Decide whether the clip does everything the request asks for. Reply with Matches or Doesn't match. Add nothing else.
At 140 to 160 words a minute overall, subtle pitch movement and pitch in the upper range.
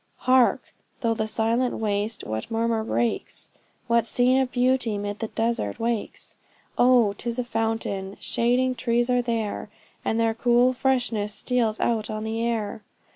Matches